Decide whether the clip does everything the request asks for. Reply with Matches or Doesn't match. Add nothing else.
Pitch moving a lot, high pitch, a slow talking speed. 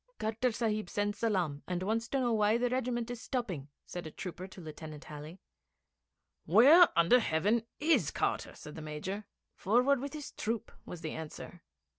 Doesn't match